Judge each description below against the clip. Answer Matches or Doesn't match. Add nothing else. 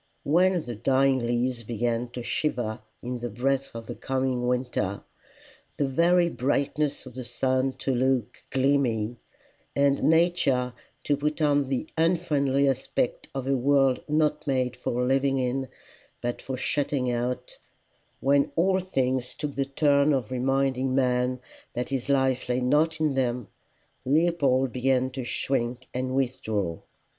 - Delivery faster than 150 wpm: Doesn't match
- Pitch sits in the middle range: Doesn't match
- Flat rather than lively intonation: Matches